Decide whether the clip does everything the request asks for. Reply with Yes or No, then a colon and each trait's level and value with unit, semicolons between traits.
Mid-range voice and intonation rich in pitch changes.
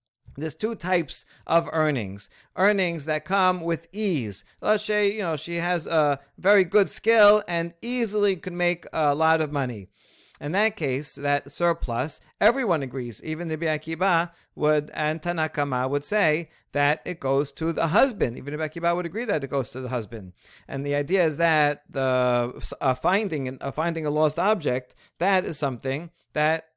No: medium, 155 Hz; average, 4.1 semitones